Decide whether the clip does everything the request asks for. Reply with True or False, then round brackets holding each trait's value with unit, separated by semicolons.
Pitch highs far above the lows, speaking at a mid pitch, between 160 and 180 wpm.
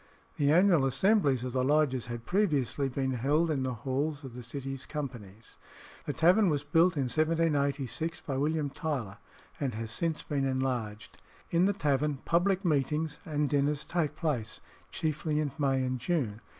False (3.4 semitones; 145 Hz; 165 wpm)